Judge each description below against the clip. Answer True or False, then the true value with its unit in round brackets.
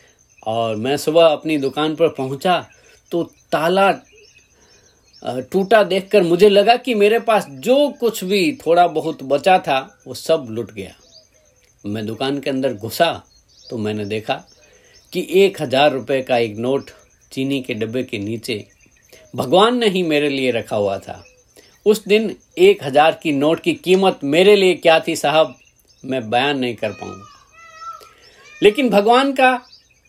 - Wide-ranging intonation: True (8.1 semitones)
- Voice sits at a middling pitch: True (160 Hz)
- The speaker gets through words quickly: False (150 wpm)